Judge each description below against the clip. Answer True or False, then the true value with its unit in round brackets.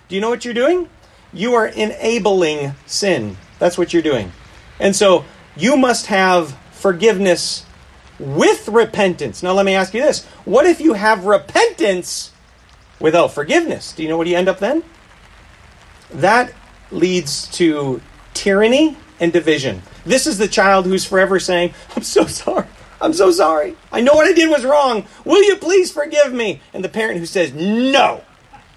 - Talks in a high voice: True (195 Hz)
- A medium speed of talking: True (165 wpm)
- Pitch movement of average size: False (6.1 semitones)